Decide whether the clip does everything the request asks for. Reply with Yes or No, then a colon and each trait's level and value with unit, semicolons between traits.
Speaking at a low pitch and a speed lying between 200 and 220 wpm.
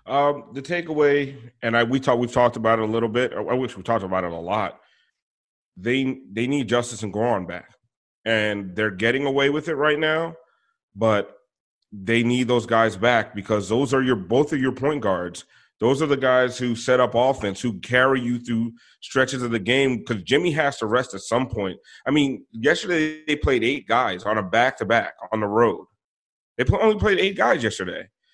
Yes: low, 120 Hz; fast, 205 wpm